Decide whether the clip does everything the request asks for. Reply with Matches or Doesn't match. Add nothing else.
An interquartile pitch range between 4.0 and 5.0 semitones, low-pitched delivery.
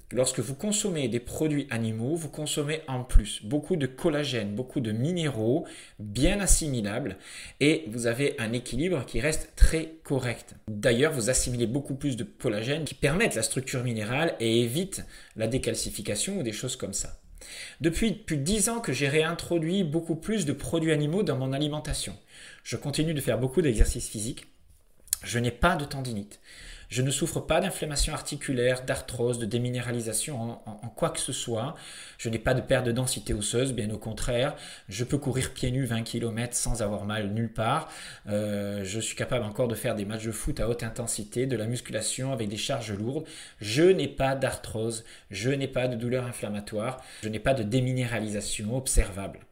Matches